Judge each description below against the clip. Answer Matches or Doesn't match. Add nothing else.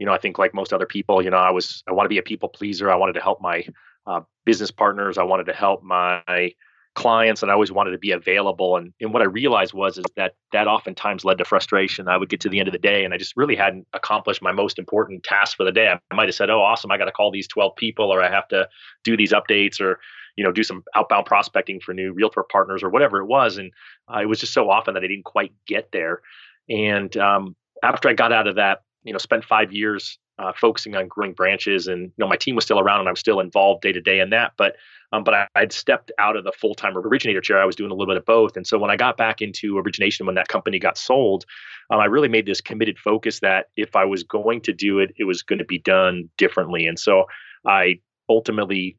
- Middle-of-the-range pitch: Doesn't match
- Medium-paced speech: Doesn't match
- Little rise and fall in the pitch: Matches